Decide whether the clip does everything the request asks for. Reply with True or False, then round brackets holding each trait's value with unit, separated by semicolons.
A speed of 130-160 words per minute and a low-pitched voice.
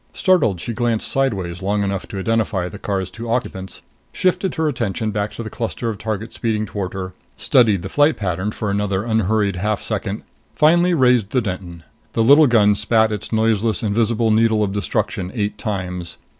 False (180 wpm; 110 Hz)